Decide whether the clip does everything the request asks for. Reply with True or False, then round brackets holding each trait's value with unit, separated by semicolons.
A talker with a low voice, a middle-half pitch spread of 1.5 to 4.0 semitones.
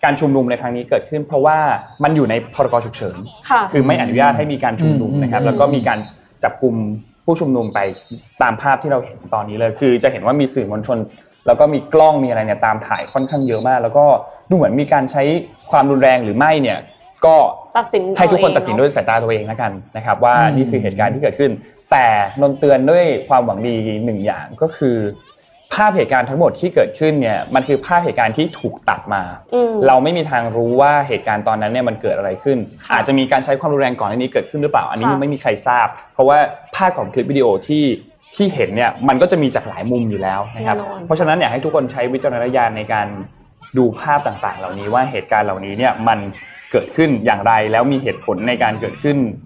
False (130 Hz; 4.4 semitones)